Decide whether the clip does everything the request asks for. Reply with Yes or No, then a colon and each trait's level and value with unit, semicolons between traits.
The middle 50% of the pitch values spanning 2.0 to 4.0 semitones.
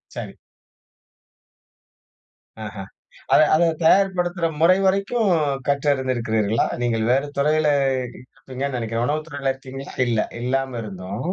No: average, 4.8 semitones